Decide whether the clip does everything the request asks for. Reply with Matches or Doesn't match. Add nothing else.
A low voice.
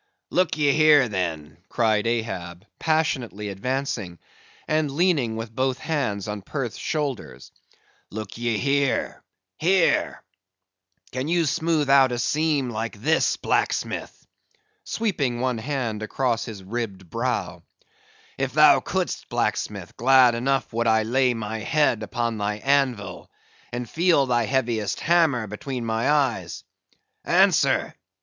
Matches